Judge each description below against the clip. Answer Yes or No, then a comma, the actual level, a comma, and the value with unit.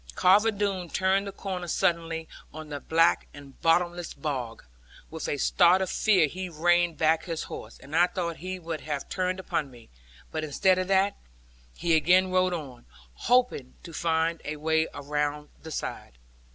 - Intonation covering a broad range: No, average, 3.2 semitones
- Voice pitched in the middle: Yes, medium, 165 Hz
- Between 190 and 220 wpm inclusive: No, average, 170 wpm